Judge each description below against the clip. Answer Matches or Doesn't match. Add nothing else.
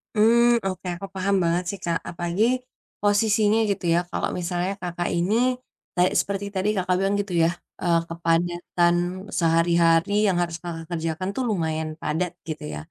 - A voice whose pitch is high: Doesn't match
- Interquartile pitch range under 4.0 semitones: Matches